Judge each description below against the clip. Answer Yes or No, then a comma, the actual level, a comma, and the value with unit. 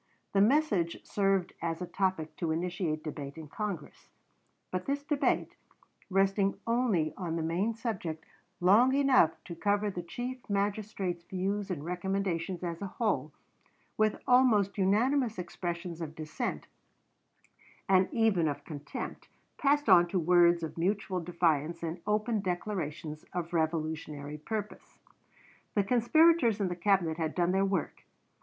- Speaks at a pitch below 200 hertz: Yes, medium, 185 Hz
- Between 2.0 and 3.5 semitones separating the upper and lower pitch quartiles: No, average, 4.0 semitones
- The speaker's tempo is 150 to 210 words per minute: No, slow, 135 wpm